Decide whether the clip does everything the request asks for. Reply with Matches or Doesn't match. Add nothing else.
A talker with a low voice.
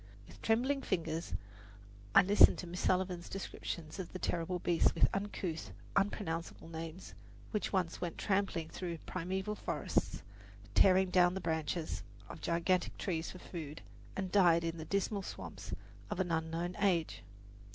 Doesn't match